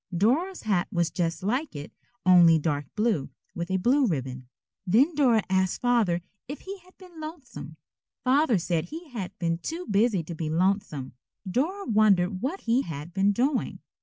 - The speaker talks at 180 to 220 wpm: No, average, 165 wpm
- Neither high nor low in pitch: No, high, 205 Hz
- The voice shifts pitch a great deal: Yes, wide, 7.7 semitones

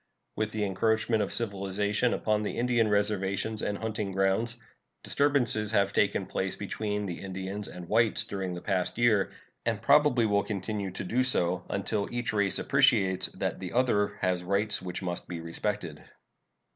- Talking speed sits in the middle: Yes, average, 160 wpm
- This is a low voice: Yes, low, 105 Hz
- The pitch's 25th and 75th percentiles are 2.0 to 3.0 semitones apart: Yes, average, 2.7 semitones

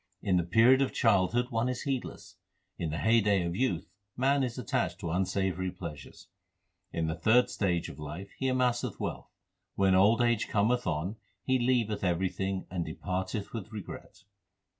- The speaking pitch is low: Yes, low, 100 Hz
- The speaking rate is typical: Yes, average, 165 wpm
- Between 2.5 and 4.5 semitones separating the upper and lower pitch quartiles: No, average, 5.0 semitones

